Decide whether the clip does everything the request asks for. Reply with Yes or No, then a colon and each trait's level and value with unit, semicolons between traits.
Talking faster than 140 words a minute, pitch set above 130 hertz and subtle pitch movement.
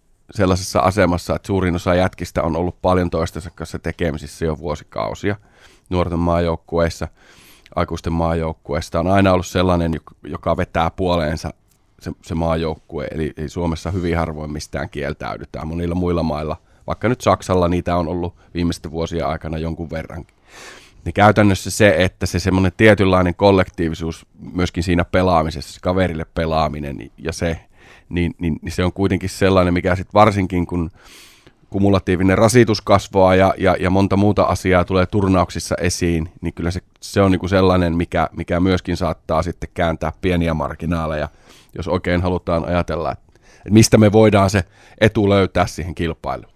No: average, 150 wpm; very low, 90 Hz; narrow, 2.3 semitones